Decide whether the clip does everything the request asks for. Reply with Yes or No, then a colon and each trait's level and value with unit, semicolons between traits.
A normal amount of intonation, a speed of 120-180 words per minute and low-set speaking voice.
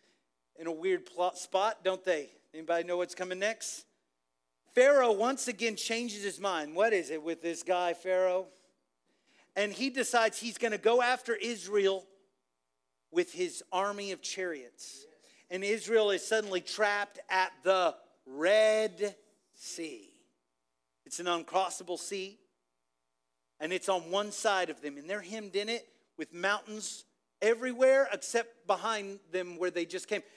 No: average, 4.3 semitones; average, 145 wpm; high, 195 Hz